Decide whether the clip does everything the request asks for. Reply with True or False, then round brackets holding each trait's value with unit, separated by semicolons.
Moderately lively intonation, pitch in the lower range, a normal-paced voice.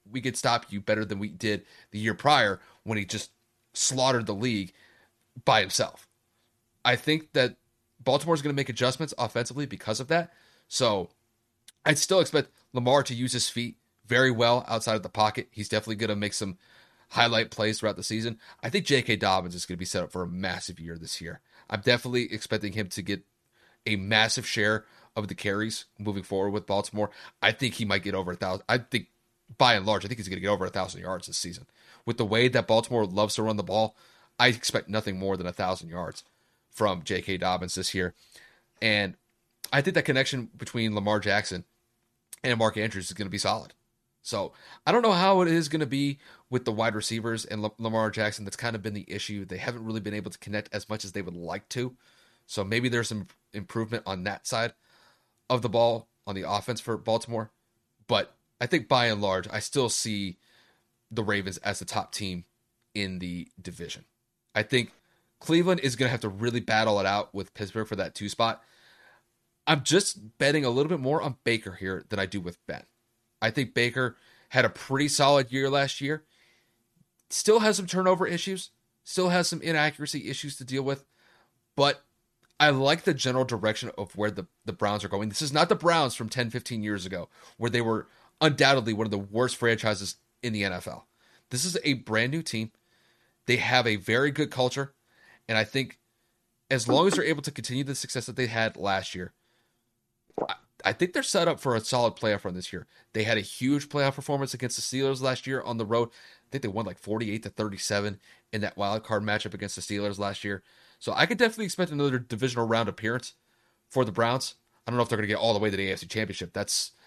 False (3.8 semitones; 115 Hz; 215 wpm)